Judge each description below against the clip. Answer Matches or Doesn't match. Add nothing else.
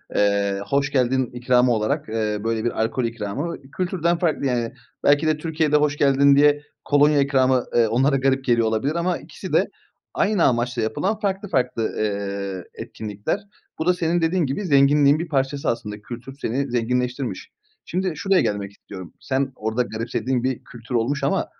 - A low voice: Matches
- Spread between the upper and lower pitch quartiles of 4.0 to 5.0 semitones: Matches